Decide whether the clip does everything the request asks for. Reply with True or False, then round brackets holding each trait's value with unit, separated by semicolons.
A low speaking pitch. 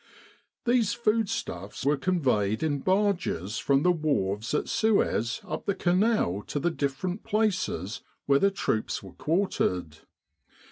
False (155 Hz)